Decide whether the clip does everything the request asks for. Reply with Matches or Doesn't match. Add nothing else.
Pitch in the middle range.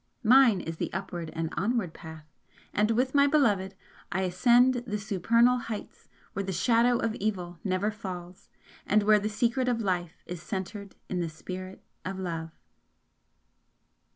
Doesn't match